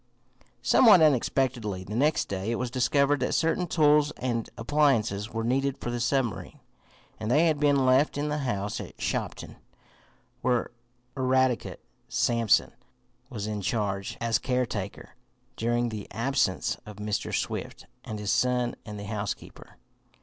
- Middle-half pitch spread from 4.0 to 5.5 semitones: Yes, average, 4.4 semitones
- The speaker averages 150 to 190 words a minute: No, average, 140 wpm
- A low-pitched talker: Yes, low, 120 Hz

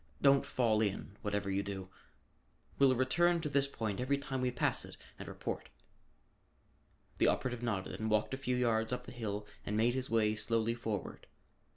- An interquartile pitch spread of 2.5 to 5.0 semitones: Yes, average, 3.4 semitones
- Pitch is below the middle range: Yes, low, 115 Hz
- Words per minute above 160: Yes, average, 180 wpm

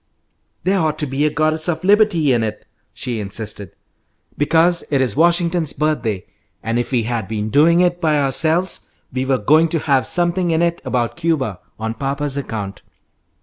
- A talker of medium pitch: Yes, medium, 145 Hz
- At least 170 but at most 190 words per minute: Yes, average, 175 wpm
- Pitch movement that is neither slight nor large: No, wide, 5.9 semitones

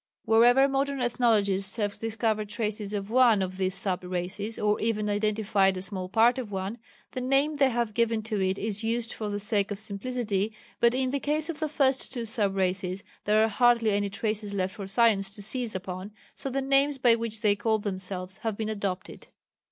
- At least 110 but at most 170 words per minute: No, average, 200 wpm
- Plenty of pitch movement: No, average, 3.2 semitones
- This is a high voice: Yes, high, 215 Hz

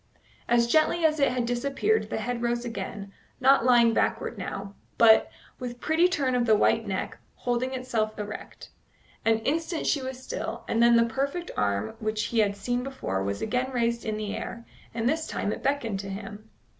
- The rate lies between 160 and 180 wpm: No, average, 190 wpm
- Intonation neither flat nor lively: Yes, average, 3.4 semitones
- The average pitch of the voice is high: Yes, high, 235 Hz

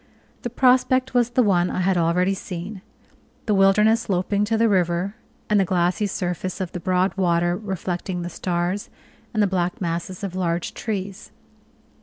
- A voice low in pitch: No, medium, 185 Hz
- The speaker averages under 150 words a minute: No, average, 165 wpm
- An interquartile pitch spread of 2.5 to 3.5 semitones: Yes, average, 2.8 semitones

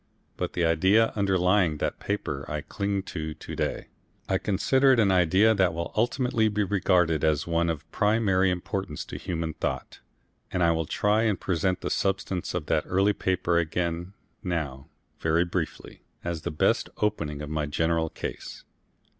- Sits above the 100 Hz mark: No, very low, 90 Hz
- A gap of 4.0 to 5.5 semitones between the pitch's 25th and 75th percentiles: No, average, 3.6 semitones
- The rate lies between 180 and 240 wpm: No, average, 165 wpm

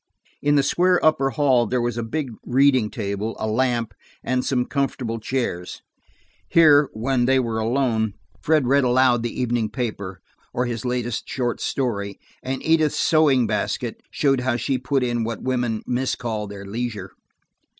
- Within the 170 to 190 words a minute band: No, average, 160 wpm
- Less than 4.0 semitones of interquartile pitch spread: Yes, average, 3.0 semitones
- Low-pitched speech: Yes, low, 125 Hz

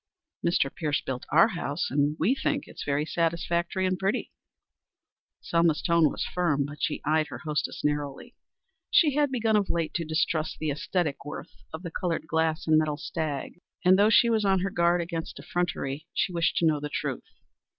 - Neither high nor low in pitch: Yes, medium, 165 Hz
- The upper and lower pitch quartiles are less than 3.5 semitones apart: Yes, average, 3.1 semitones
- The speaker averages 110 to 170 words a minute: No, average, 185 wpm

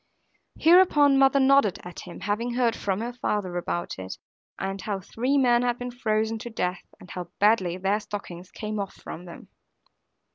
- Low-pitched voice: No, high, 215 Hz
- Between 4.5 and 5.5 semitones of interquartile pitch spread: Yes, average, 4.8 semitones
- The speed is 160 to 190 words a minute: Yes, average, 175 wpm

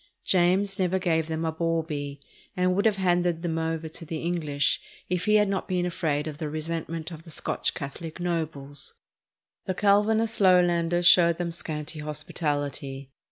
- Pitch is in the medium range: Yes, medium, 165 Hz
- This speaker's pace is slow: No, average, 165 wpm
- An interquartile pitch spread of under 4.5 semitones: Yes, narrow, 2.6 semitones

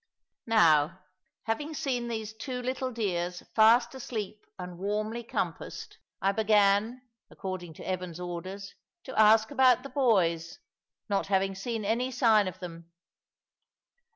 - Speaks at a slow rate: Yes, slow, 125 wpm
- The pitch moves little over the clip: No, average, 4.3 semitones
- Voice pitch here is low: No, high, 215 Hz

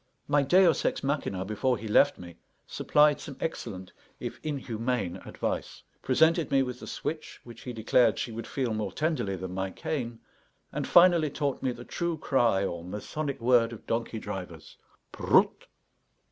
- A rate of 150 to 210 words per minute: Yes, average, 160 wpm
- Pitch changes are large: Yes, wide, 5.7 semitones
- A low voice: Yes, low, 120 Hz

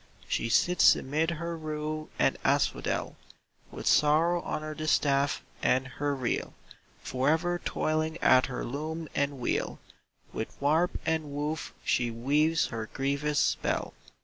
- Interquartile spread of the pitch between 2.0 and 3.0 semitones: Yes, narrow, 2.6 semitones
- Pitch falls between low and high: Yes, medium, 150 Hz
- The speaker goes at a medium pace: No, slow, 130 wpm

